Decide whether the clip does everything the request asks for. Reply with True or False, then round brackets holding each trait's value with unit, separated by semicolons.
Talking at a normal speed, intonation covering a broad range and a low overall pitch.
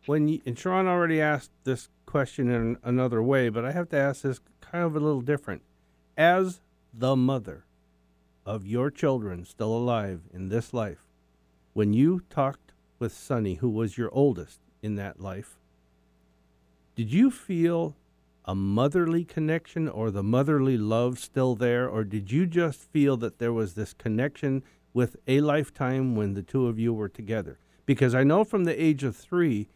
True (170 wpm; 6.2 semitones; 120 Hz)